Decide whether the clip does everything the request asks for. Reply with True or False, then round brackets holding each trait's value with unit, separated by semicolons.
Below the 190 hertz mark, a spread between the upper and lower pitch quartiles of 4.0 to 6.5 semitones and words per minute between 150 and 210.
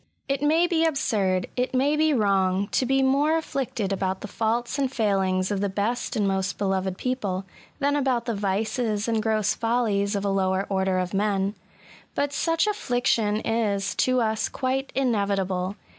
False (215 Hz; 4.9 semitones; 175 wpm)